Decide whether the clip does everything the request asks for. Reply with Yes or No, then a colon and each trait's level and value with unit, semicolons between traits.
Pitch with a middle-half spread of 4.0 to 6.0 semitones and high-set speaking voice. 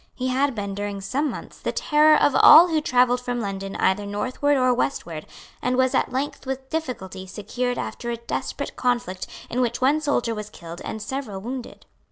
Yes: average, 4.6 semitones; high, 245 Hz